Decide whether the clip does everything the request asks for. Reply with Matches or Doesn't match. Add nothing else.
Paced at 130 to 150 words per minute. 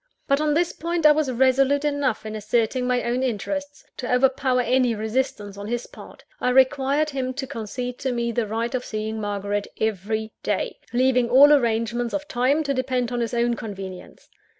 Doesn't match